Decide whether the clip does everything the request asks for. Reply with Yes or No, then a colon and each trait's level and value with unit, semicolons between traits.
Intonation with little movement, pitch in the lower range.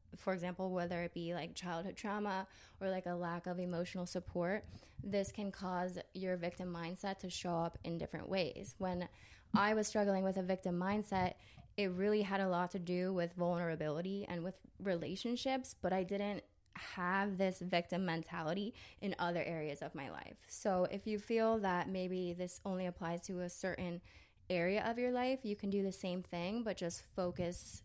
No: narrow, 2.1 semitones; medium, 185 Hz